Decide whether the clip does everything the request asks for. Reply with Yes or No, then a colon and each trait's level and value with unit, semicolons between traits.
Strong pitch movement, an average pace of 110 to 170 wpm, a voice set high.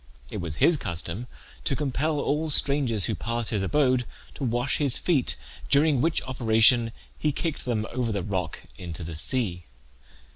No: wide, 5.7 semitones; average, 160 wpm; low, 120 Hz